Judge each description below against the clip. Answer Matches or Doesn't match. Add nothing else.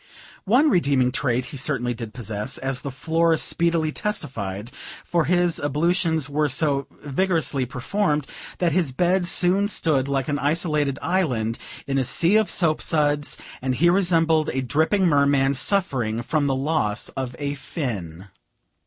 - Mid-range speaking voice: Matches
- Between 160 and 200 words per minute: Doesn't match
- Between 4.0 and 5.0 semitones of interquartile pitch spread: Matches